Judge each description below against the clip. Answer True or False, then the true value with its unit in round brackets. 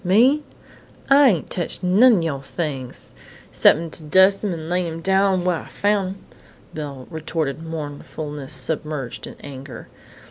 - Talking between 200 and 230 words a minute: False (150 wpm)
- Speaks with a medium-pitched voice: True (165 Hz)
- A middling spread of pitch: True (4.5 semitones)